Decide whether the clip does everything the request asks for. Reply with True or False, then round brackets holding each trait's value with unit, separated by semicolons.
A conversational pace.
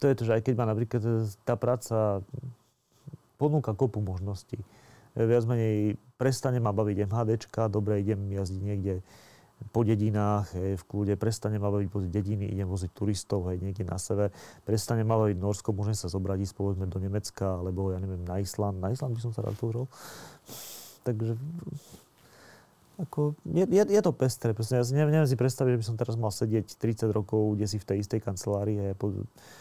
False (190 wpm)